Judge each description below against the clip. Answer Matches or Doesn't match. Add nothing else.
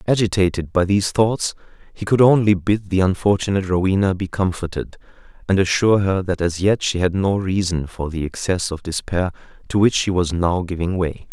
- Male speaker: Matches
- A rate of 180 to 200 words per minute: Matches